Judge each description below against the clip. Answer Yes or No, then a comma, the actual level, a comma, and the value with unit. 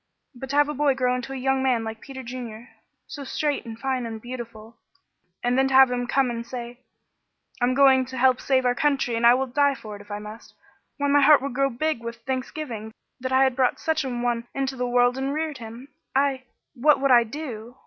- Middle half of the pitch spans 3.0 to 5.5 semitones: No, narrow, 2.4 semitones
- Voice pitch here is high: Yes, very high, 255 Hz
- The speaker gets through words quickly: Yes, fast, 230 wpm